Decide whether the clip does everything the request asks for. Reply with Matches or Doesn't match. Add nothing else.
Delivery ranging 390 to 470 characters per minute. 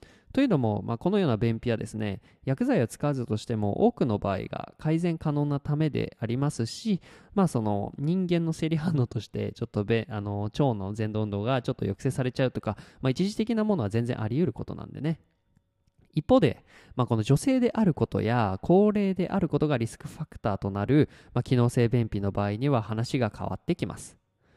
Matches